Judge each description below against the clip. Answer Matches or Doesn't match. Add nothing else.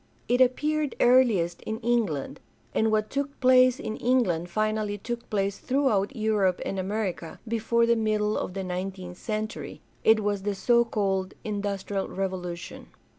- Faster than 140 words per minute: Matches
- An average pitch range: Matches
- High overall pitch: Matches